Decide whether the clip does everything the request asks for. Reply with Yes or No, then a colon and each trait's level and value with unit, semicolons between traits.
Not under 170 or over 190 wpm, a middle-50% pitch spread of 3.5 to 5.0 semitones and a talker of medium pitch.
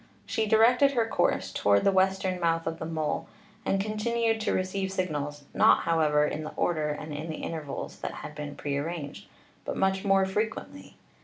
Yes: average, 180 wpm; average, 4.7 semitones; medium, 175 Hz